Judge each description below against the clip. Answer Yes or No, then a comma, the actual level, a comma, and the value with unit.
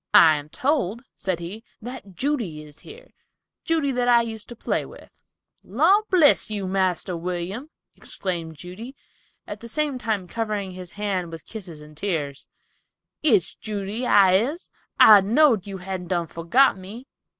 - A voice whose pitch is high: Yes, high, 200 Hz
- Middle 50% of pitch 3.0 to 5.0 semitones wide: No, wide, 5.4 semitones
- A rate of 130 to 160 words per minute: Yes, average, 155 wpm